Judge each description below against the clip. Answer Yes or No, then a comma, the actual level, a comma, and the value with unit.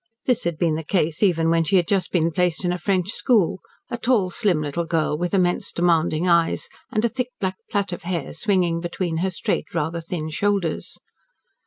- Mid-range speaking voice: Yes, medium, 175 Hz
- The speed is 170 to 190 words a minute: No, average, 200 wpm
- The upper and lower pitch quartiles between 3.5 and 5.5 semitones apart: No, average, 2.8 semitones